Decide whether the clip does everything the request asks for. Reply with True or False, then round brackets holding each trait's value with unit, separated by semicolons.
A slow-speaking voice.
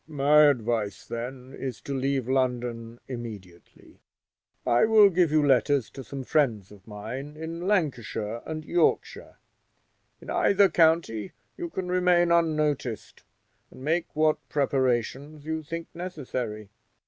True (125 wpm)